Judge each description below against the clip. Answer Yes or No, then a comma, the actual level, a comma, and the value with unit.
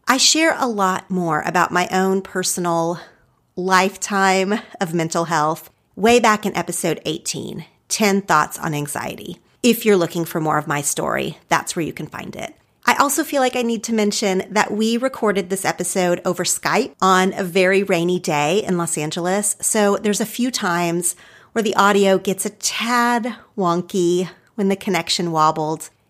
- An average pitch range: Yes, average, 3.3 semitones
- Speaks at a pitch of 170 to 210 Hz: Yes, high, 190 Hz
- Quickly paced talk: No, average, 170 wpm